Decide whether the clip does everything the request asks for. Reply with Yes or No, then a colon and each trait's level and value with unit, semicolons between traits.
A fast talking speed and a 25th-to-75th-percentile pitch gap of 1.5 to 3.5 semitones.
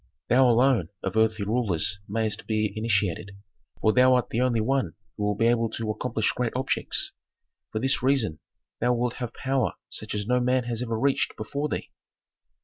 No: average, 180 wpm; average, 2.8 semitones